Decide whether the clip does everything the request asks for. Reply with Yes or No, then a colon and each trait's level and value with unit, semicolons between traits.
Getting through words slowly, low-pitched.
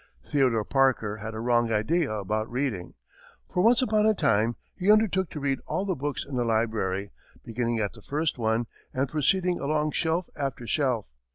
No: average, 180 wpm; low, 130 Hz